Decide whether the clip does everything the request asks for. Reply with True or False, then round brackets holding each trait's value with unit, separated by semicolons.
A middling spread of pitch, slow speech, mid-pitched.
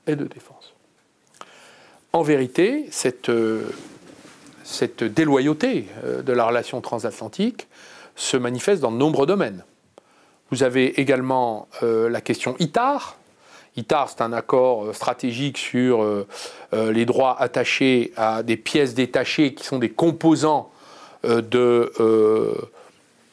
False (3.5 semitones; 130 wpm; 125 Hz)